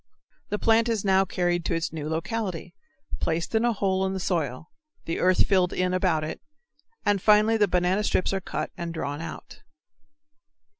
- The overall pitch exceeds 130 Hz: Yes, medium, 185 Hz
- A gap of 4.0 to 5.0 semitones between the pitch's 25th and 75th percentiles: No, average, 3.6 semitones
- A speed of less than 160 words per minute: No, average, 180 wpm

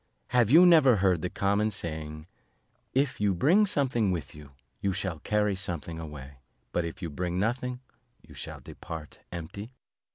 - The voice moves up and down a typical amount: No, wide, 6.6 semitones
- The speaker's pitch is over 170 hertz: No, very low, 95 Hz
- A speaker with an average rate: Yes, average, 160 wpm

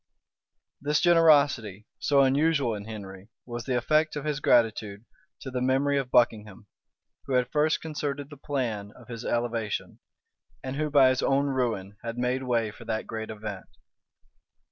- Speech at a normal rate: Yes, average, 160 wpm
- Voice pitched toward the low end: Yes, low, 125 Hz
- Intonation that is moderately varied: Yes, average, 4.3 semitones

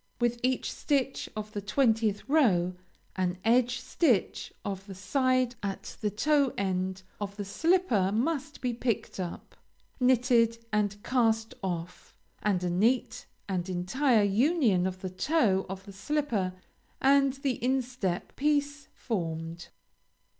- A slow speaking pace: Yes, slow, 130 wpm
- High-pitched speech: Yes, high, 225 Hz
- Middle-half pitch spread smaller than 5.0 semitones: No, wide, 5.4 semitones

